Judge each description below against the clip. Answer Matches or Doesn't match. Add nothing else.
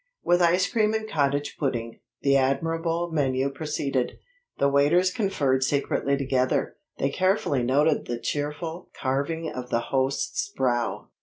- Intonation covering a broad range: Doesn't match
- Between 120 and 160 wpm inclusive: Matches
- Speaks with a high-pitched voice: Doesn't match